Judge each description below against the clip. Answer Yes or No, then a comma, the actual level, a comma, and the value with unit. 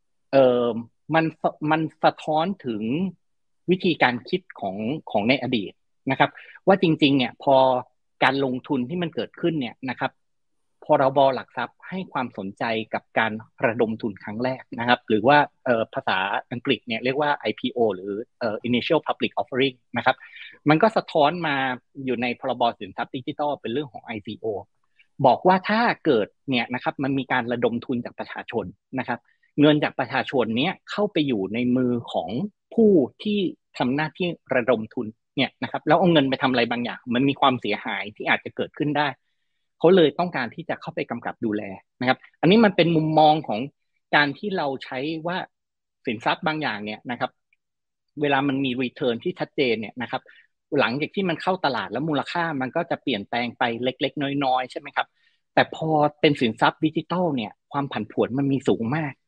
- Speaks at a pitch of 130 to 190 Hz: Yes, medium, 140 Hz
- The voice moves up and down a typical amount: Yes, average, 4.3 semitones